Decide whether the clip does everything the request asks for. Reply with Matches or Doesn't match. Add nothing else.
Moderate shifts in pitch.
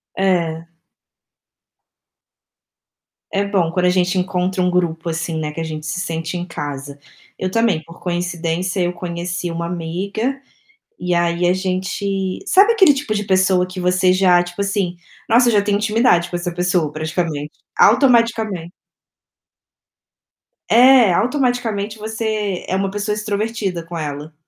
Matches